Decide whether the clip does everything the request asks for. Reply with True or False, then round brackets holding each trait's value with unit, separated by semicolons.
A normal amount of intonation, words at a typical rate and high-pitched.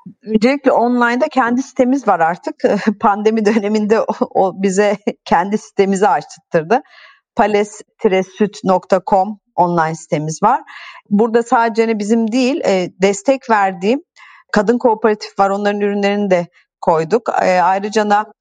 True (3.3 semitones; 110 wpm; 210 Hz)